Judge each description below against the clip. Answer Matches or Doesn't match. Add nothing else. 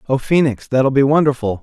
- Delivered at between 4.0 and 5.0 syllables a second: Doesn't match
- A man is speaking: Matches